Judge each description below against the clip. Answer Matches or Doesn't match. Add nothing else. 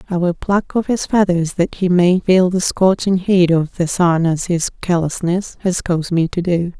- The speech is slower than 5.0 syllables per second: Matches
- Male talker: Doesn't match